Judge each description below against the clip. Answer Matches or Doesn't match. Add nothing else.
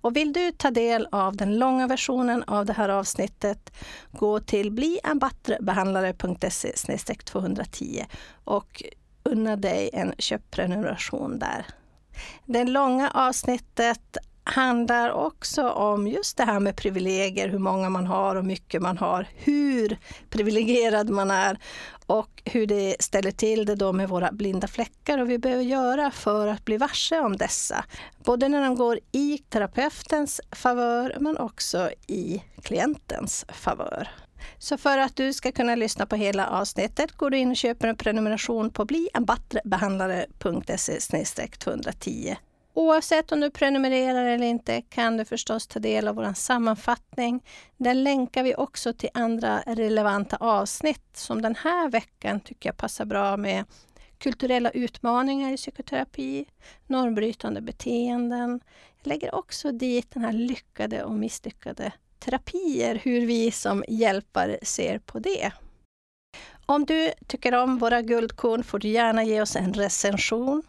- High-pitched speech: Matches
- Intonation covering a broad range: Doesn't match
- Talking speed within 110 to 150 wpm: Matches